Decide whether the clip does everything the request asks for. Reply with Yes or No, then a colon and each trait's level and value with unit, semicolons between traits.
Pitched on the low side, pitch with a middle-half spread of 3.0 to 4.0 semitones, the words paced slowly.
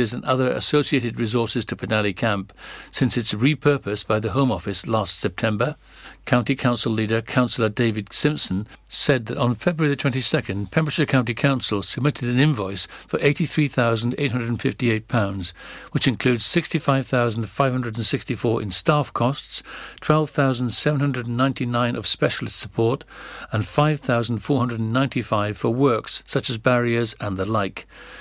Yes: low, 120 Hz; average, 3.7 semitones; slow, 120 wpm